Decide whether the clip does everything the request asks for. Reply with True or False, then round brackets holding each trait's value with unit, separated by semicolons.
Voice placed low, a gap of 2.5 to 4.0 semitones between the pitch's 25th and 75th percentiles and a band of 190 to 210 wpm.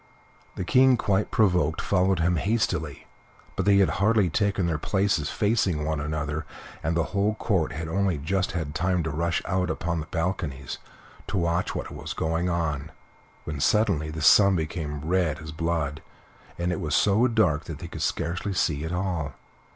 False (85 Hz; 3.7 semitones; 180 wpm)